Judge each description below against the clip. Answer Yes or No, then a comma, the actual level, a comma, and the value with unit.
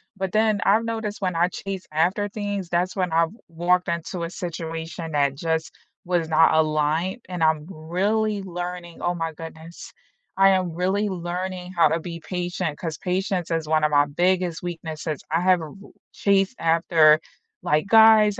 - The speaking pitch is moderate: Yes, medium, 175 Hz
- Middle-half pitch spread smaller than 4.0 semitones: Yes, average, 2.7 semitones